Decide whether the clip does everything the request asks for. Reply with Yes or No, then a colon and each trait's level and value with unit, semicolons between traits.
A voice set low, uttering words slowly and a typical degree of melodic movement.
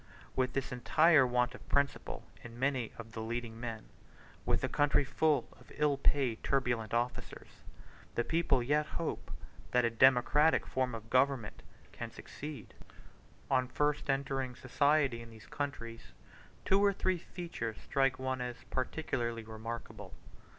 No: low, 130 Hz; average, 145 wpm; average, 3.5 semitones